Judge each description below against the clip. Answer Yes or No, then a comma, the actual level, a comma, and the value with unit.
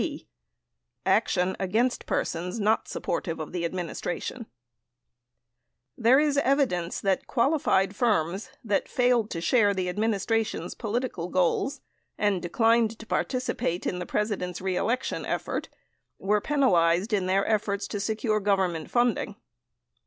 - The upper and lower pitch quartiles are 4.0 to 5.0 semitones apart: Yes, average, 4.4 semitones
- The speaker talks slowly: Yes, slow, 130 wpm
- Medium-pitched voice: No, high, 205 Hz